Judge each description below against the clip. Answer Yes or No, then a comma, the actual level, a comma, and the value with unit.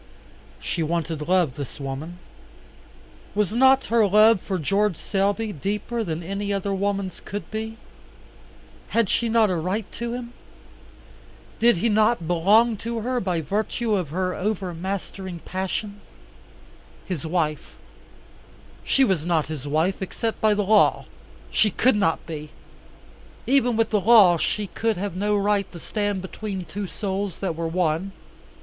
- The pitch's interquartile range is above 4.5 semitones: No, average, 3.7 semitones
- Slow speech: No, average, 145 wpm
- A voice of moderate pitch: No, high, 195 Hz